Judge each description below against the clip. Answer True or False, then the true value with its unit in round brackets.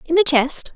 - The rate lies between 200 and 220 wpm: False (235 wpm)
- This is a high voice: True (310 Hz)